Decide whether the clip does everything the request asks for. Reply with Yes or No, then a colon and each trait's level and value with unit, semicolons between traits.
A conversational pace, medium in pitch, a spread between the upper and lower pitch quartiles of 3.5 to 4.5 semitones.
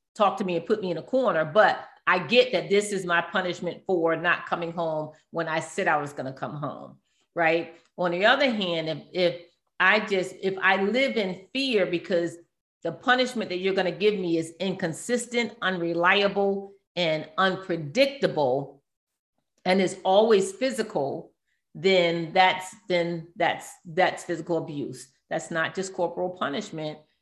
No: average, 165 wpm; medium, 180 Hz; average, 2.9 semitones